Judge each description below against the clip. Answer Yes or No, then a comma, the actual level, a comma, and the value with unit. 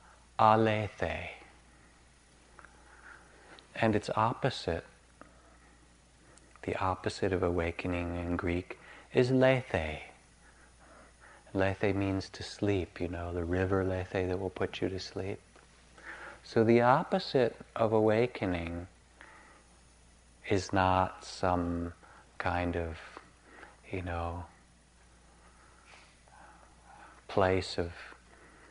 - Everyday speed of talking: No, slow, 85 wpm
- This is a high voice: No, very low, 90 Hz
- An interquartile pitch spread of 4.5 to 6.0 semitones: Yes, wide, 5.5 semitones